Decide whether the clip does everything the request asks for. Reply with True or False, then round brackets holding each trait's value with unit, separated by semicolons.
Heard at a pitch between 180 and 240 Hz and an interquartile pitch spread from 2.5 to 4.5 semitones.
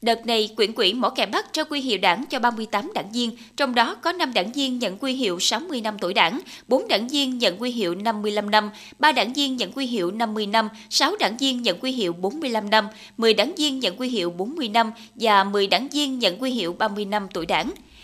True (235 Hz; 4.2 semitones)